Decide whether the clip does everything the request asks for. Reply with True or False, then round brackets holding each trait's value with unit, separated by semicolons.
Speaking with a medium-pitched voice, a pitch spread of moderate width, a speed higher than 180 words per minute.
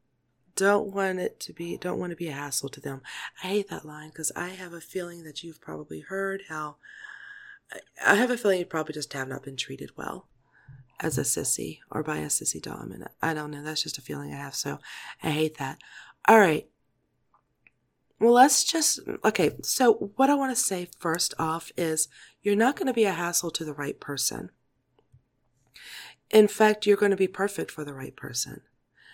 False (170 Hz; 6.0 semitones; 200 wpm)